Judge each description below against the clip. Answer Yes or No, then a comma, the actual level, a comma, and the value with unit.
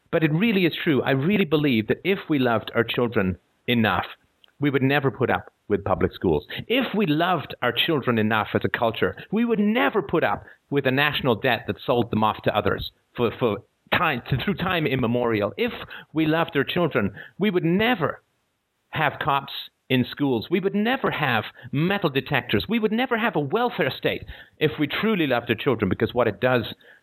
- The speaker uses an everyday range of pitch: No, wide, 7.5 semitones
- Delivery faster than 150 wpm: Yes, average, 195 wpm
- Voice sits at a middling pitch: Yes, medium, 145 Hz